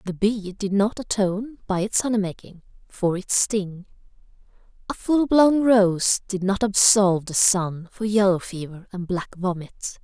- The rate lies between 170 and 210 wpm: No, average, 160 wpm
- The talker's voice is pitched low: No, high, 200 Hz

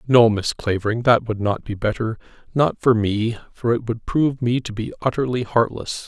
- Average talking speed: Yes, average, 190 wpm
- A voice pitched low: Yes, low, 115 Hz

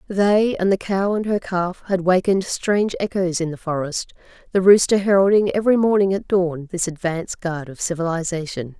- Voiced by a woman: Yes, female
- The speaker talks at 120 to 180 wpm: Yes, average, 175 wpm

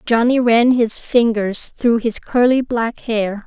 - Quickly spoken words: No, average, 155 wpm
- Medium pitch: No, high, 230 Hz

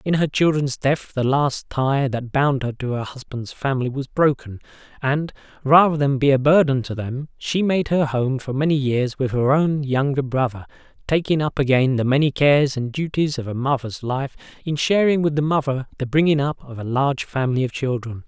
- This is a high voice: No, low, 135 Hz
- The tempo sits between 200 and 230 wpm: Yes, fast, 205 wpm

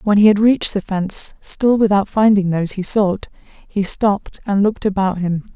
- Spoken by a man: No, female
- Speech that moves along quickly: No, average, 195 wpm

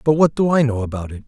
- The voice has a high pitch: No, low, 130 Hz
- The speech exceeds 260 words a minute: Yes, fast, 330 wpm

